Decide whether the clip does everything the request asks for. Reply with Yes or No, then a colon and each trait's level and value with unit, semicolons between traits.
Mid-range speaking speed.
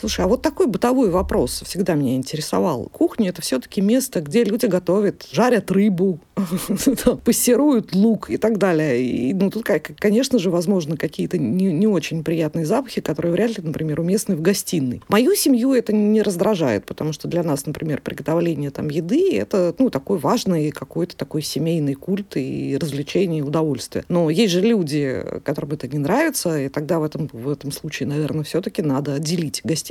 No: fast, 165 wpm